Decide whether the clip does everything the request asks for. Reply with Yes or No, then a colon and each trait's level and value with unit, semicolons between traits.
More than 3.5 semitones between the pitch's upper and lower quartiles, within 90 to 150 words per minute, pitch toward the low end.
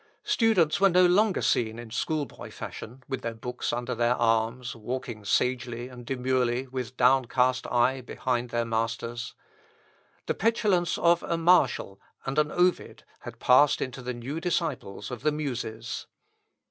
Yes: average, 4.1 semitones; average, 145 wpm; low, 125 Hz